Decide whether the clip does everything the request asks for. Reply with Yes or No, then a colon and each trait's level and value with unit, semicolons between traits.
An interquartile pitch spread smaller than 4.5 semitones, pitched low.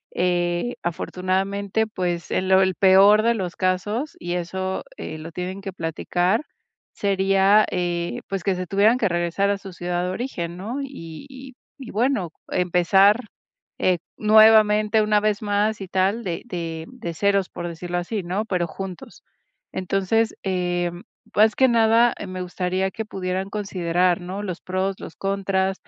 No: average, 2.9 semitones; high, 190 Hz